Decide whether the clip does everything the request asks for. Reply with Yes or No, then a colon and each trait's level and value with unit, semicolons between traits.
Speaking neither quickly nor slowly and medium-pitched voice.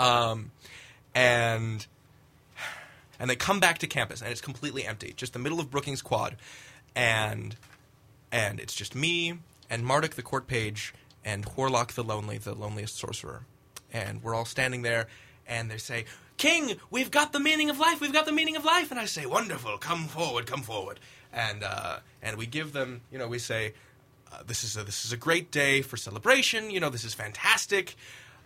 No: average, 190 wpm; low, 125 Hz